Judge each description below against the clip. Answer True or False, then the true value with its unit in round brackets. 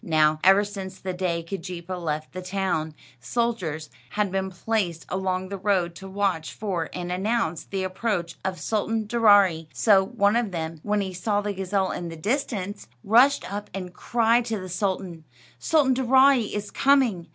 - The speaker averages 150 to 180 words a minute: True (170 wpm)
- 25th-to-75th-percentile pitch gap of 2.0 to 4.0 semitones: True (3.2 semitones)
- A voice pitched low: False (190 Hz)